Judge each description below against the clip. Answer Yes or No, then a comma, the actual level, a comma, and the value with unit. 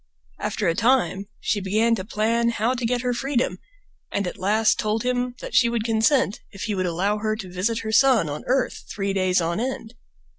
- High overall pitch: Yes, high, 220 Hz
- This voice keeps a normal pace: No, fast, 210 wpm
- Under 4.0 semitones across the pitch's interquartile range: Yes, average, 3.5 semitones